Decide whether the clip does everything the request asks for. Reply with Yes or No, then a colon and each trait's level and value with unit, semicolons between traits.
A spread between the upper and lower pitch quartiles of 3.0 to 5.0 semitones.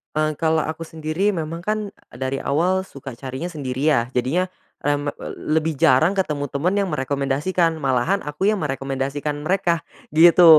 Yes: average, 3.5 semitones